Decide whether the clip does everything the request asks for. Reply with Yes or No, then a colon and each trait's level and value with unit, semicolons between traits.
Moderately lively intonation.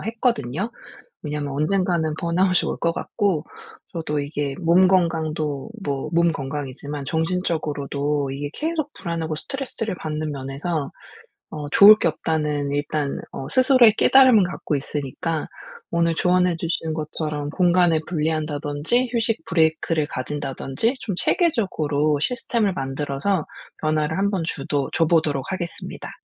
Yes: average, 3.9 semitones